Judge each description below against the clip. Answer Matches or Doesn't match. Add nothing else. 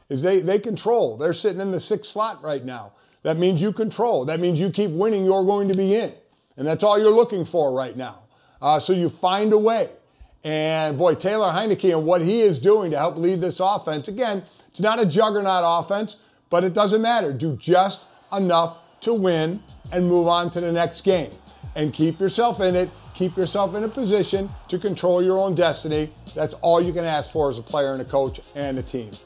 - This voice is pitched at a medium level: Matches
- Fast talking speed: Matches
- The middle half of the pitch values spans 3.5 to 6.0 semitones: Matches